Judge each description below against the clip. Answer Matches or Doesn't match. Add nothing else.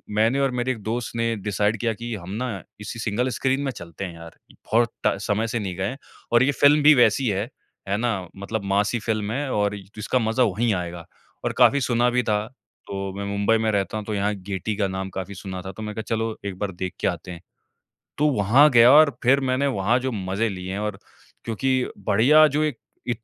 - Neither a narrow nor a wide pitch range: Matches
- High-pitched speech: Doesn't match